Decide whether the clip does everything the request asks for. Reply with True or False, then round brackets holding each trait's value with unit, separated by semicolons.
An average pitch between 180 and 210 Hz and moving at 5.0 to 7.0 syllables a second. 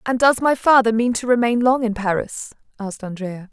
False (230 Hz; 5.4 syllables/s)